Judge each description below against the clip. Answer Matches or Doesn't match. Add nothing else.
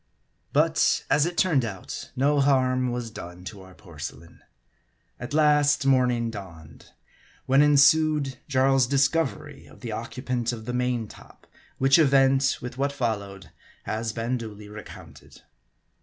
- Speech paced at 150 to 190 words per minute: Doesn't match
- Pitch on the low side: Matches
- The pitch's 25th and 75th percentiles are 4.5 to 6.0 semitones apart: Doesn't match